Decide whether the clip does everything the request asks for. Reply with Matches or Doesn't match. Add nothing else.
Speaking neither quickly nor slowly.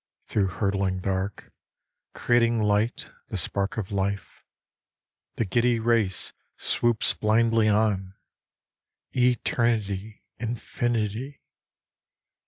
Doesn't match